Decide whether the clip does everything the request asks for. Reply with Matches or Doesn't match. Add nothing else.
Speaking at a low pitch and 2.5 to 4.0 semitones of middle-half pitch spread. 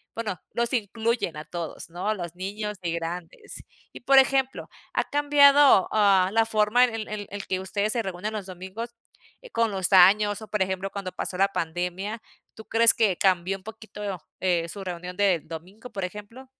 Doesn't match